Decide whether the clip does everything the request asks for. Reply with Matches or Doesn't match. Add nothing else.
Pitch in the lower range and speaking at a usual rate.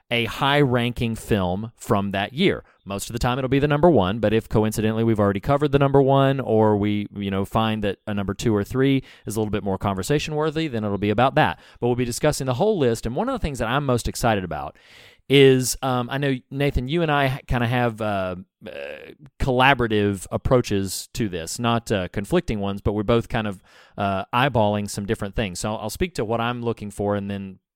Doesn't match